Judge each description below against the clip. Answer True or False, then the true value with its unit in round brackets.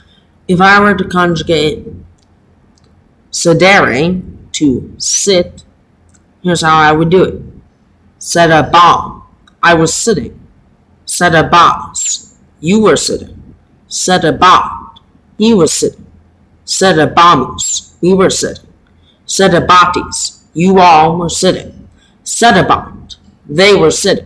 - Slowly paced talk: True (100 wpm)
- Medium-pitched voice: True (170 Hz)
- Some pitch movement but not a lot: True (3.4 semitones)